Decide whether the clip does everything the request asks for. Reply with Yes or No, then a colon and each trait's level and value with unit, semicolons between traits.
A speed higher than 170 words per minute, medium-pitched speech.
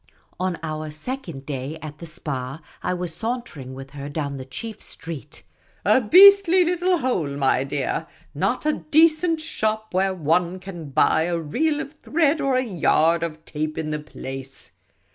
Yes: average, 180 wpm; medium, 170 Hz